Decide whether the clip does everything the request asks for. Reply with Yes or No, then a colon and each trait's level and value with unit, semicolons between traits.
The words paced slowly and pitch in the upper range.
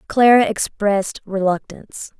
Yes: slow, 80 wpm; high, 210 Hz